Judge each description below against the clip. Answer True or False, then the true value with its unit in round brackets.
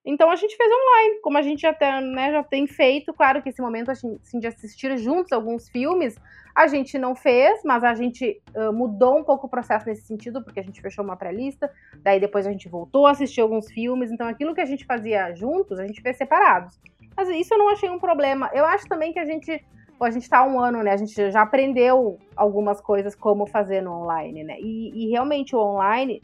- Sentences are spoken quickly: True (230 wpm)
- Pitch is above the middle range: True (250 Hz)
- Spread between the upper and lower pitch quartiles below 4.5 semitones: False (5.2 semitones)